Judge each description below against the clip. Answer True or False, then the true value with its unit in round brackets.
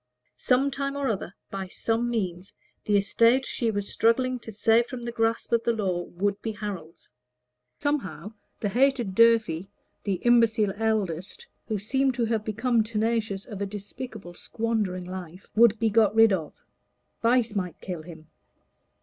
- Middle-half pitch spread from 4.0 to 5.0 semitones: False (3.2 semitones)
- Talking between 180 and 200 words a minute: False (160 wpm)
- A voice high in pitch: True (220 Hz)